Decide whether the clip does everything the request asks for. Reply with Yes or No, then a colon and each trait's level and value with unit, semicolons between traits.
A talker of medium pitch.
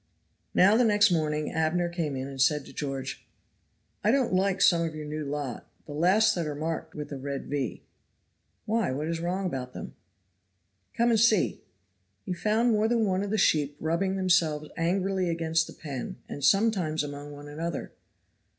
Yes: medium, 165 Hz